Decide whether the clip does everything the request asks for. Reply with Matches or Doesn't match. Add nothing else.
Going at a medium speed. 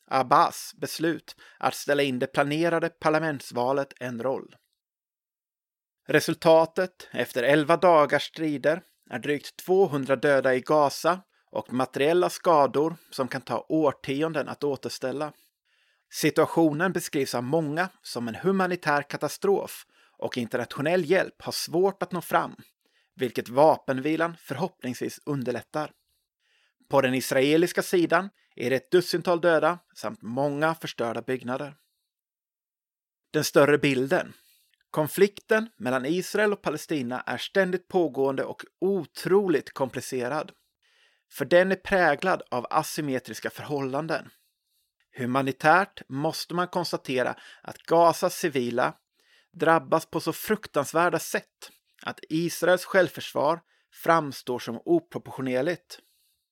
Doesn't match